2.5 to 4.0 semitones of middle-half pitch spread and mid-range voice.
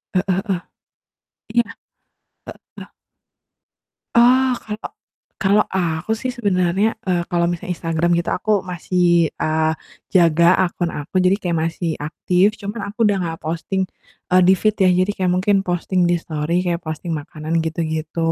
Yes: average, 2.9 semitones; medium, 175 Hz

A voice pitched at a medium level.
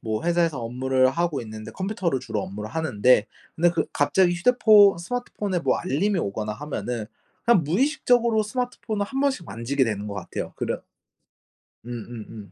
Yes: medium, 160 Hz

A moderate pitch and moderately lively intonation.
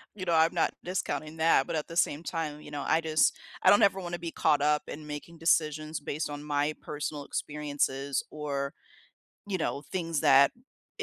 No: medium, 150 Hz; narrow, 2.2 semitones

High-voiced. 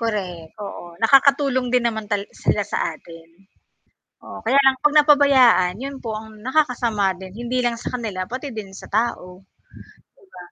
Yes: high, 230 Hz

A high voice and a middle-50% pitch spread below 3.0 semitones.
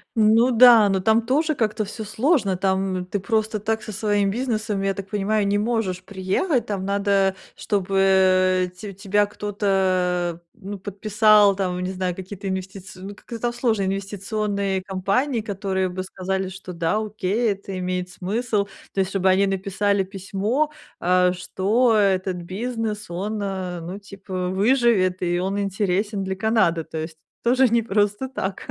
Yes: high, 195 Hz; narrow, 2.4 semitones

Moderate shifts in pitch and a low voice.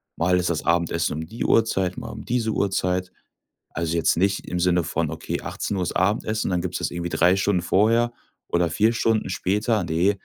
Yes: average, 3.3 semitones; very low, 90 Hz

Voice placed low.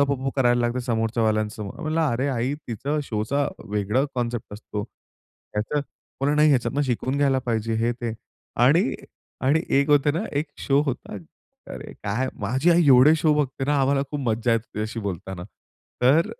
Yes: low, 125 Hz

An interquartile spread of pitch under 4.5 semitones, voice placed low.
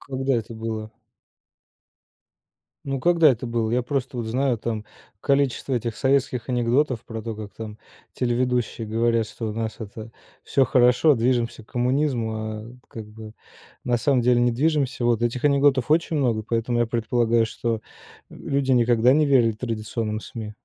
Yes: average, 2.7 semitones; low, 120 Hz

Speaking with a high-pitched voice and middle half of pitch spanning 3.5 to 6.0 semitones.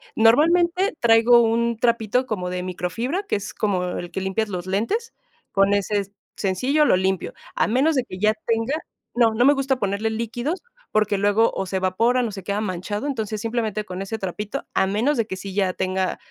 Yes: high, 215 Hz; average, 4.0 semitones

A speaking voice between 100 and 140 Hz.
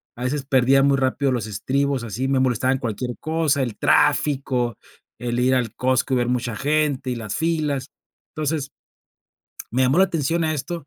Yes: low, 135 Hz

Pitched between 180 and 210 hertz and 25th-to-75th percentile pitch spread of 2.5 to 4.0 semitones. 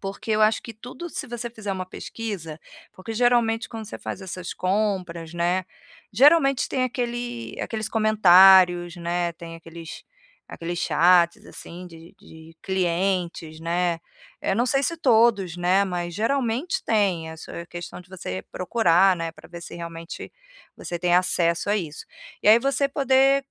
No: medium, 185 Hz; average, 4.9 semitones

